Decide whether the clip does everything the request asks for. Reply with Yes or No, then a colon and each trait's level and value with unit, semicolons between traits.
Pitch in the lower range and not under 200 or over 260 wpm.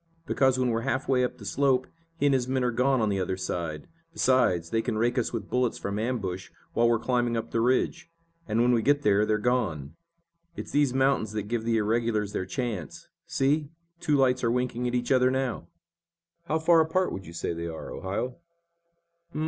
Yes: low, 120 Hz; fast, 205 wpm